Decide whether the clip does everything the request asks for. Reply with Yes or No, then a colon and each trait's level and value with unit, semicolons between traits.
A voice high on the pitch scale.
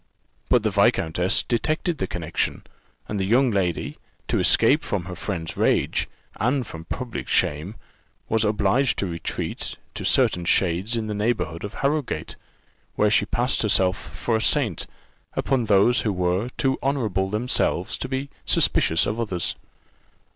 No: low, 105 Hz